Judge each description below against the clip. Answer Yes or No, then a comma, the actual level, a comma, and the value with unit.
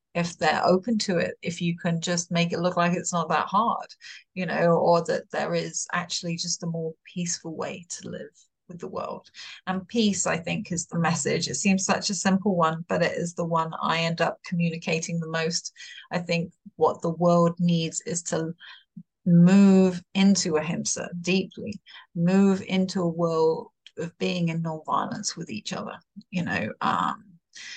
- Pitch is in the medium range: Yes, medium, 175 Hz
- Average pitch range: No, narrow, 2.1 semitones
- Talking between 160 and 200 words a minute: Yes, average, 180 wpm